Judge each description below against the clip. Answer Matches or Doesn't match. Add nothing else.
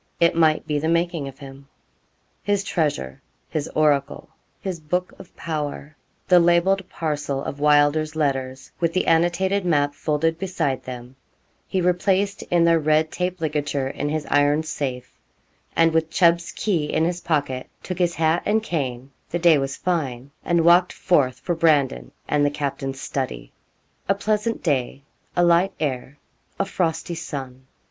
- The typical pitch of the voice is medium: Matches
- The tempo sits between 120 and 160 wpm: Matches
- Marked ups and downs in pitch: Doesn't match